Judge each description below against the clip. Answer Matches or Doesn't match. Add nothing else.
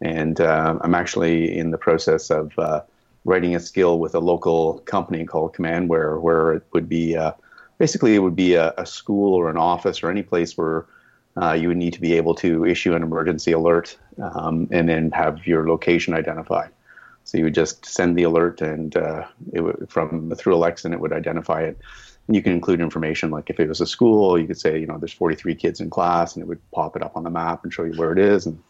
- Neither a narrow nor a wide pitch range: Doesn't match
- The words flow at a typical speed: Doesn't match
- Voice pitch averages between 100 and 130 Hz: Doesn't match